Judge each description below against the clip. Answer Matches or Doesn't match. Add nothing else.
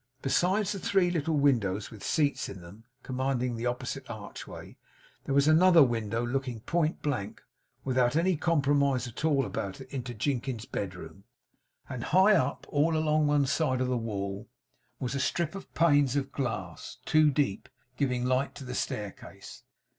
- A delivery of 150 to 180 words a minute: Matches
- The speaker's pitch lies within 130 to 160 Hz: Matches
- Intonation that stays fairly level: Doesn't match